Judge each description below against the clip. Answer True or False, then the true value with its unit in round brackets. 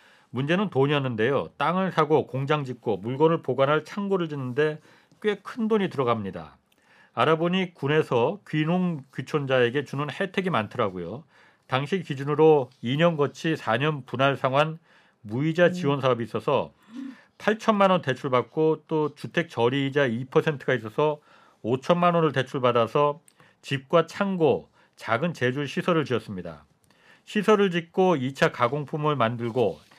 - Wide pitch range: False (4.9 semitones)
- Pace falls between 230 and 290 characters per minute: True (285 characters per minute)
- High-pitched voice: False (150 Hz)